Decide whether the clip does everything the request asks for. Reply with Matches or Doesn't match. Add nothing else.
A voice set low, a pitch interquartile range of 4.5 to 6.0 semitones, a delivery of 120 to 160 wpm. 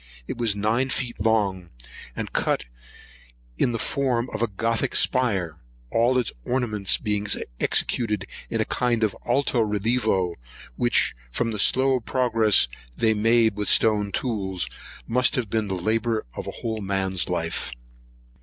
Doesn't match